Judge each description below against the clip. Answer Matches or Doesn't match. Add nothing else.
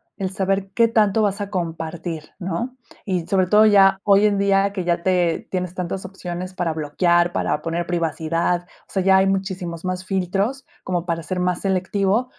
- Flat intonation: Matches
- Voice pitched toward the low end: Doesn't match